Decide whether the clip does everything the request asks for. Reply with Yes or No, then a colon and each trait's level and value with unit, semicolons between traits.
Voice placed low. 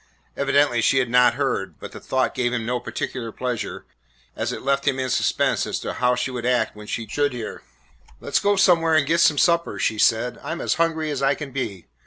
Yes: low, 130 Hz